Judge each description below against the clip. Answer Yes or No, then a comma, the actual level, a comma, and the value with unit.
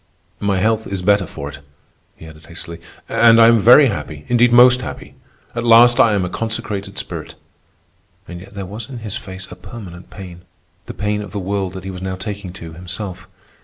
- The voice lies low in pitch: Yes, low, 100 Hz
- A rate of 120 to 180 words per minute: No, average, 200 wpm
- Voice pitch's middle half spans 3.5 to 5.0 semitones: Yes, average, 3.9 semitones